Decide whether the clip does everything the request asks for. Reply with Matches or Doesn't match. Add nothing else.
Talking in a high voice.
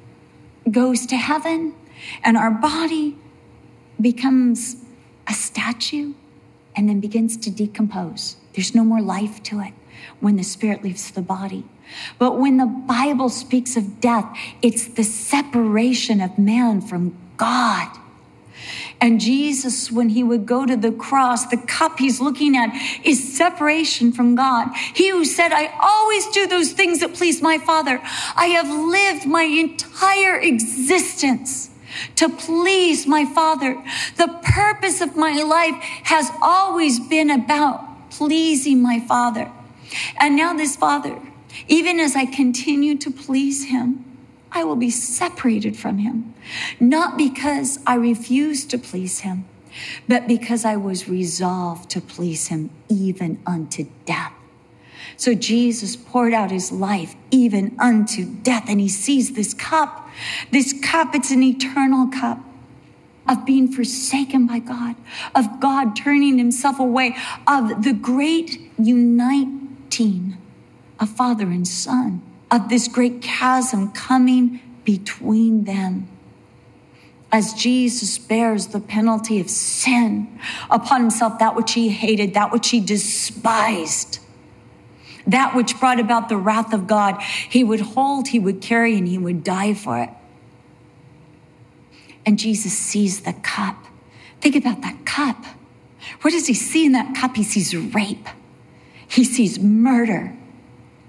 Matches